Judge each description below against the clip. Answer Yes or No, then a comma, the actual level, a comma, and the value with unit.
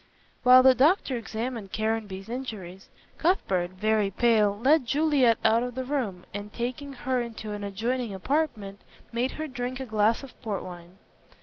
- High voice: Yes, high, 230 Hz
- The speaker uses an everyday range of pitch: Yes, average, 4.1 semitones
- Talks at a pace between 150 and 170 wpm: Yes, average, 160 wpm